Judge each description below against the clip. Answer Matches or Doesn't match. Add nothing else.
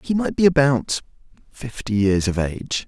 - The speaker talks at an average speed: Matches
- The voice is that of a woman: Doesn't match